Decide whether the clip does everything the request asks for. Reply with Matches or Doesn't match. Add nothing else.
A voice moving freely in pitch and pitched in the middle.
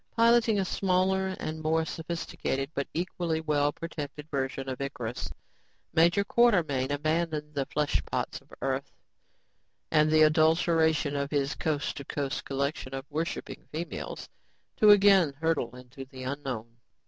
Doesn't match